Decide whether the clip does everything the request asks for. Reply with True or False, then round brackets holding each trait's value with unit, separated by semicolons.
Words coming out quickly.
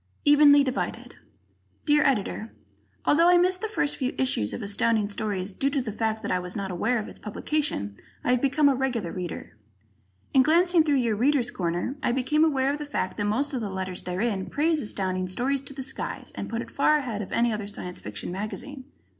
True (210 wpm)